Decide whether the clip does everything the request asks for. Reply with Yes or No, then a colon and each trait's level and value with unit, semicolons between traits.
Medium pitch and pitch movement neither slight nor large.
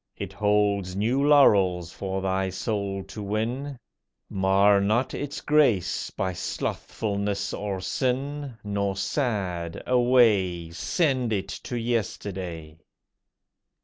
No: low, 100 Hz; average, 4.2 semitones